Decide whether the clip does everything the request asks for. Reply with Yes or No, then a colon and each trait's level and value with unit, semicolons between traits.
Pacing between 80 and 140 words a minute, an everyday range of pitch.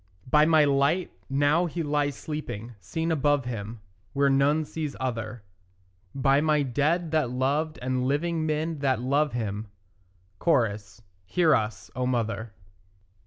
Yes: slow, 135 wpm; average, 3.9 semitones